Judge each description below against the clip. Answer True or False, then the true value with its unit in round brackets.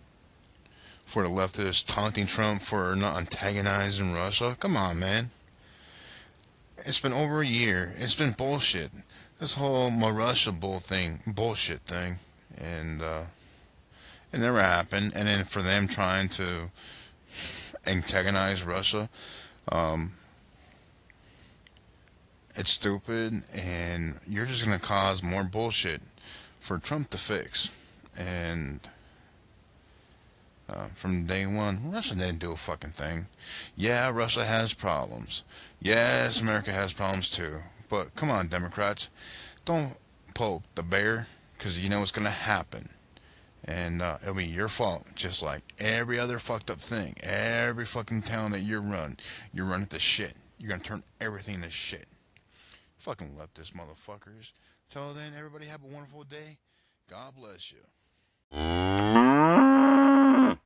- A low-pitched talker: True (100 Hz)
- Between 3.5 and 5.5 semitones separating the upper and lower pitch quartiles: True (4.2 semitones)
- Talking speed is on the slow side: True (130 wpm)